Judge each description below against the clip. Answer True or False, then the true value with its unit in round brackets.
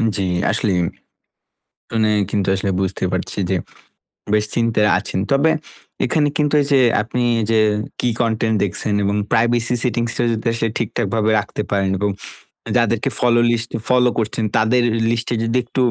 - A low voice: True (115 Hz)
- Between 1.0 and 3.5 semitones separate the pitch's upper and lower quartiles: True (2.6 semitones)